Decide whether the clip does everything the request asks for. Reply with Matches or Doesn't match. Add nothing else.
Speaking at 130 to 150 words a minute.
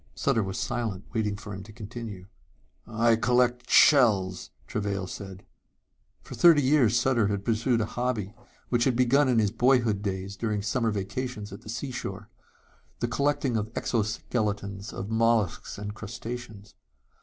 Matches